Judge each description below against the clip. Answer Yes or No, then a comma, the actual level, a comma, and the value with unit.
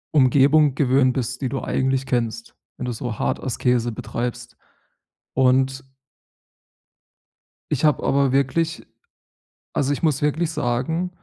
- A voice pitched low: Yes, low, 130 Hz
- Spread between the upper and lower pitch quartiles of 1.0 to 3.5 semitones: Yes, narrow, 2.6 semitones